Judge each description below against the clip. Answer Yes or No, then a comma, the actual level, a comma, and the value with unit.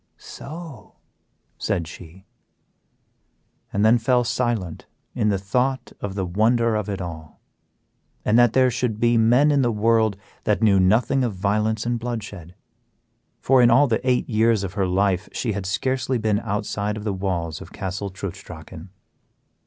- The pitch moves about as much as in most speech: Yes, average, 3.7 semitones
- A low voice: Yes, low, 110 Hz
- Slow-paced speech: No, average, 160 wpm